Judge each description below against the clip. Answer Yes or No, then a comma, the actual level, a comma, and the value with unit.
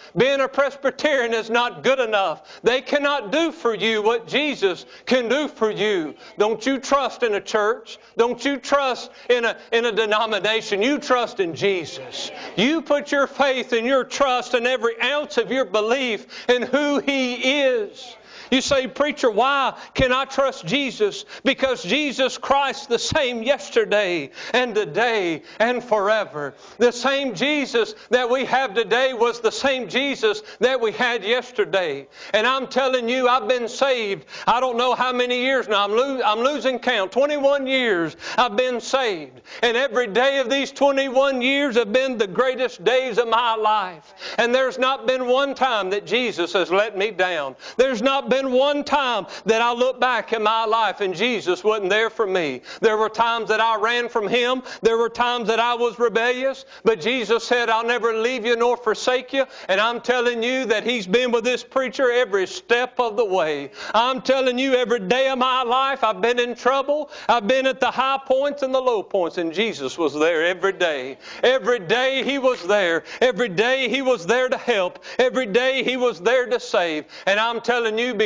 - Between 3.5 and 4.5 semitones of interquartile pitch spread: No, average, 2.8 semitones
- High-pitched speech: Yes, high, 245 Hz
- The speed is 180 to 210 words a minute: Yes, average, 190 wpm